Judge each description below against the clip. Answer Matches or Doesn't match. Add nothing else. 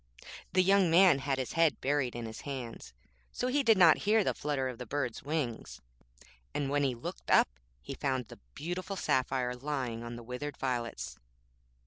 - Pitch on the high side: Doesn't match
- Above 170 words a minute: Matches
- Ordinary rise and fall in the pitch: Matches